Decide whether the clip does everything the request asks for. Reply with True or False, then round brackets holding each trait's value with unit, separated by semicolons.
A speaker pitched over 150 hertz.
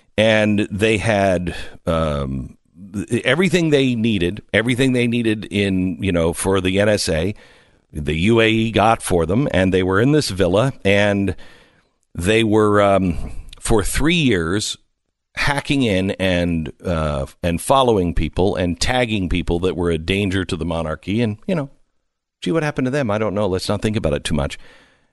False (100 Hz)